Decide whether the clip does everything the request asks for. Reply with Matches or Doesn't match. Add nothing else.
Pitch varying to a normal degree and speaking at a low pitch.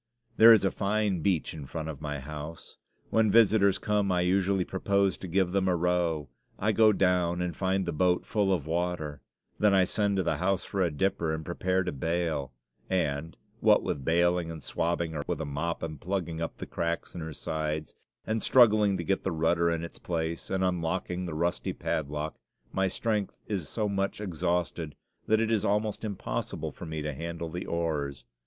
Matches